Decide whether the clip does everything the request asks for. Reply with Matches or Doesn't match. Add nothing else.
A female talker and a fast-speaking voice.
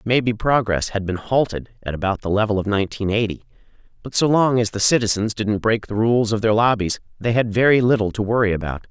Doesn't match